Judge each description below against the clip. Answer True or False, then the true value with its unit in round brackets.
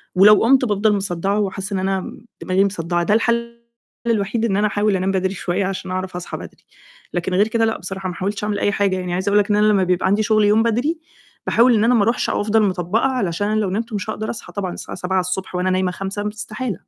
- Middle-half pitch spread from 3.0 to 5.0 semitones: False (2.5 semitones)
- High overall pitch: True (200 Hz)